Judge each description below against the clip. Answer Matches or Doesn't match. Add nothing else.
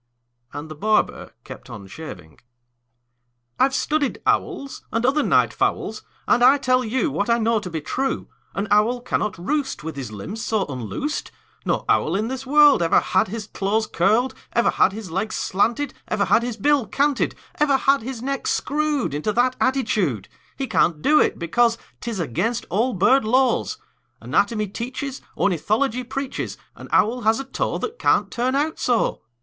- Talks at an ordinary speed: Matches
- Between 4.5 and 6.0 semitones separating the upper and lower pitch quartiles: Matches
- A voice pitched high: Matches